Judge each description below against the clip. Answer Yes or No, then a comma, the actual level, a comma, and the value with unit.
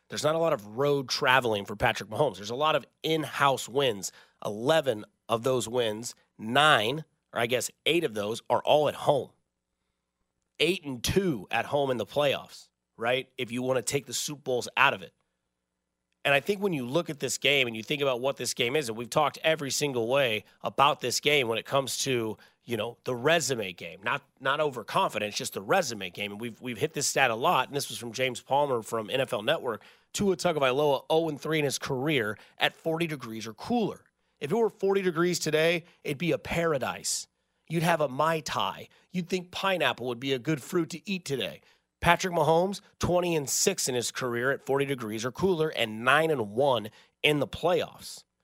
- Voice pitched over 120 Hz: Yes, medium, 140 Hz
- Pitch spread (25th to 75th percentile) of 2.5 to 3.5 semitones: No, average, 5.2 semitones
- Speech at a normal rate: No, fast, 210 wpm